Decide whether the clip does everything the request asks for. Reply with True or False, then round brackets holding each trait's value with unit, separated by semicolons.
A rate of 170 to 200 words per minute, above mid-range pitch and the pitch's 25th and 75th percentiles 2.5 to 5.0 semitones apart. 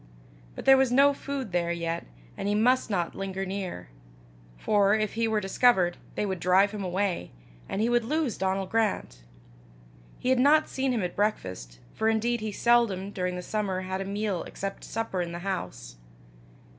True (180 wpm; 200 Hz; 3.7 semitones)